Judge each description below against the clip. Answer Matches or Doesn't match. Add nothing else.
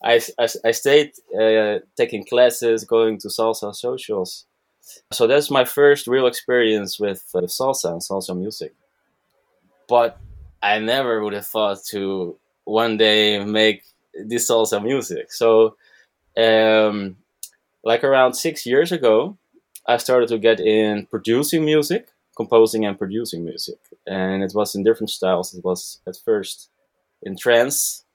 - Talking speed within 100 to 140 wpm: Matches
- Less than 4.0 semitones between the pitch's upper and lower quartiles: Matches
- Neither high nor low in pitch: Doesn't match